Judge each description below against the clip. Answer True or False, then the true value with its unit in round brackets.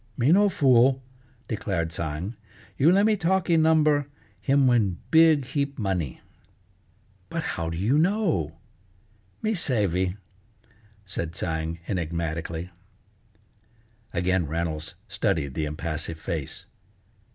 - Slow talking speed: True (105 wpm)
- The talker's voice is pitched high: False (95 Hz)